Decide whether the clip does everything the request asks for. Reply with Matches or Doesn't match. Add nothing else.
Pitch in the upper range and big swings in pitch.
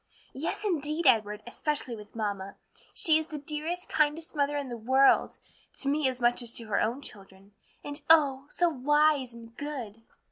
Doesn't match